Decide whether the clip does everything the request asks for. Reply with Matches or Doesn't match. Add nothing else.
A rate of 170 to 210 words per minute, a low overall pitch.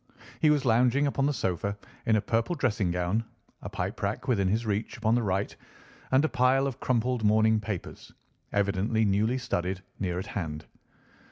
Matches